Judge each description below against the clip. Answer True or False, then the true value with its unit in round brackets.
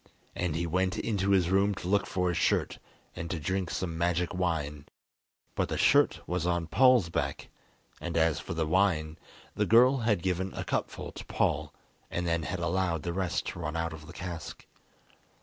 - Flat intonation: True (2.3 semitones)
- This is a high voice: False (85 Hz)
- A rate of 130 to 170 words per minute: False (190 wpm)